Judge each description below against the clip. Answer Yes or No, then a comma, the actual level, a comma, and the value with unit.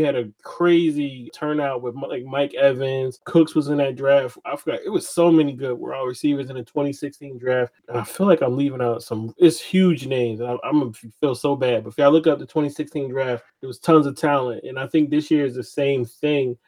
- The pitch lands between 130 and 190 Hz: Yes, medium, 140 Hz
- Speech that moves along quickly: Yes, fast, 235 wpm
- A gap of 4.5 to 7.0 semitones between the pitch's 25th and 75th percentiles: No, average, 3.3 semitones